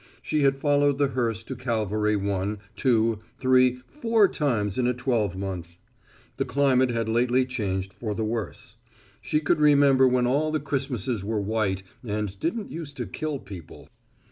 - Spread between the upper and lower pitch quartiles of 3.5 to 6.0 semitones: Yes, average, 4.7 semitones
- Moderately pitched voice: No, low, 125 Hz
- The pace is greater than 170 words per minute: No, average, 160 wpm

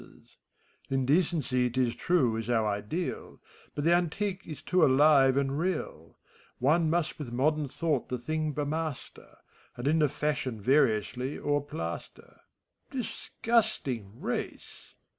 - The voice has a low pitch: No, medium, 145 Hz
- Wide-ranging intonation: No, average, 4.2 semitones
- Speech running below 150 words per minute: Yes, average, 140 wpm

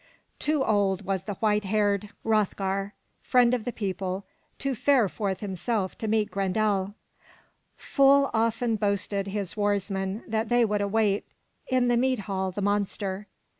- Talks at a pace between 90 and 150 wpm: Yes, average, 145 wpm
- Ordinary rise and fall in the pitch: No, narrow, 2.3 semitones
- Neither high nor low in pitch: No, high, 205 Hz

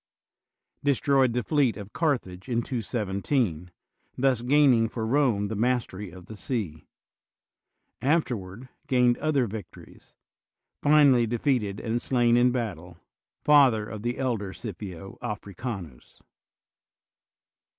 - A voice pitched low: Yes, low, 120 Hz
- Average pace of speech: No, slow, 110 wpm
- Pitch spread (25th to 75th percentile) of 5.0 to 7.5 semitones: No, average, 4.5 semitones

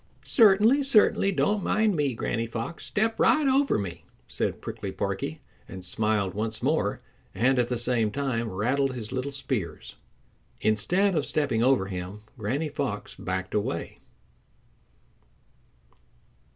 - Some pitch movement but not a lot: No, wide, 7.4 semitones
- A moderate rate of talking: No, slow, 130 wpm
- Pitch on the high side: No, low, 125 Hz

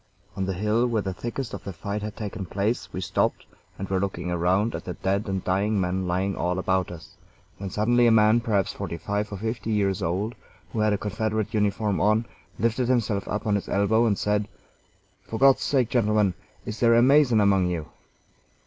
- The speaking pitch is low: Yes, low, 105 Hz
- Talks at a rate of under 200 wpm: No, fast, 205 wpm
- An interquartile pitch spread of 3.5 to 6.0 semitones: No, average, 2.7 semitones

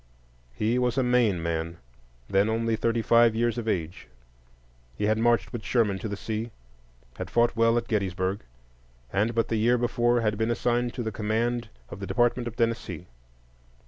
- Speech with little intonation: Yes, narrow, 2.1 semitones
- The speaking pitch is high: No, low, 115 Hz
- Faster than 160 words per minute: Yes, average, 175 wpm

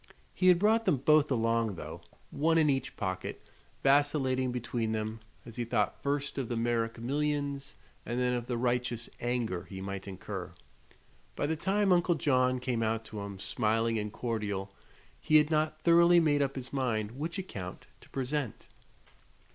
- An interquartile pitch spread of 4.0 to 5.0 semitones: Yes, average, 4.7 semitones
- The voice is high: No, low, 125 Hz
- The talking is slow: No, average, 170 wpm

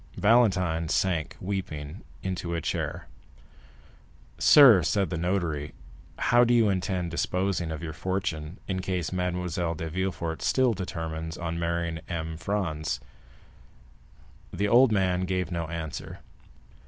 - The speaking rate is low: Yes, slow, 125 wpm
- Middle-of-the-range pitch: No, very low, 90 Hz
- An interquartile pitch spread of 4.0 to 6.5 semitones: No, average, 2.7 semitones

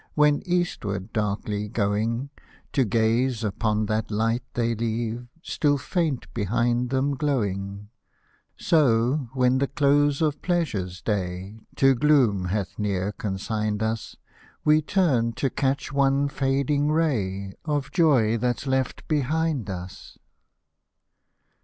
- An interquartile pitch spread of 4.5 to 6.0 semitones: Yes, average, 5.2 semitones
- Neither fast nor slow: No, slow, 120 wpm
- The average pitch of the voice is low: Yes, low, 120 Hz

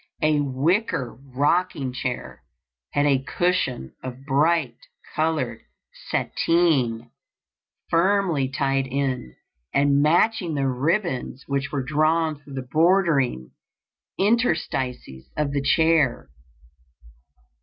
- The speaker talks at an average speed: No, slow, 95 wpm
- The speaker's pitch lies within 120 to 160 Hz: Yes, medium, 140 Hz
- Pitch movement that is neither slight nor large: Yes, average, 4.1 semitones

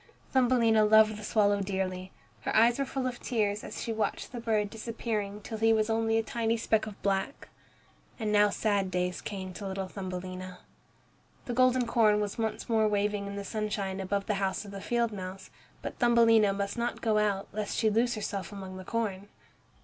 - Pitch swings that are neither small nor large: No, narrow, 2.3 semitones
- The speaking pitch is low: No, high, 210 Hz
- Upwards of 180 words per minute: Yes, average, 195 wpm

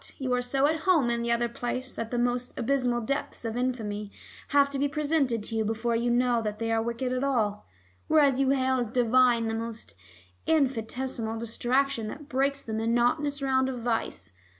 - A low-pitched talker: No, high, 245 Hz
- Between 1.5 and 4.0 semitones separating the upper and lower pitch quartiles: Yes, average, 3.0 semitones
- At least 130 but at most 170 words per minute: No, average, 190 wpm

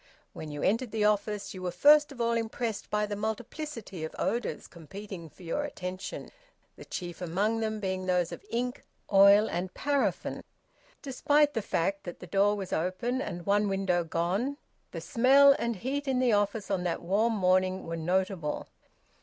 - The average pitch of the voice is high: Yes, high, 205 Hz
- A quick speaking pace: No, average, 175 wpm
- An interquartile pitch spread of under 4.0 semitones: No, average, 4.3 semitones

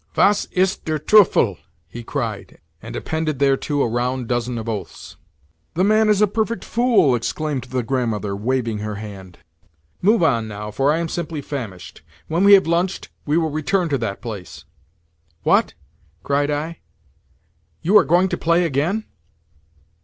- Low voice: No, medium, 145 Hz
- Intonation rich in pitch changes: Yes, wide, 6.8 semitones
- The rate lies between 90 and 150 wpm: No, average, 160 wpm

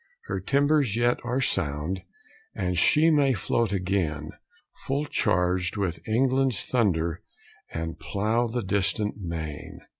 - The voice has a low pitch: Yes, low, 100 Hz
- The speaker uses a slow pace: Yes, slow, 120 wpm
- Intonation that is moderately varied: No, wide, 6.1 semitones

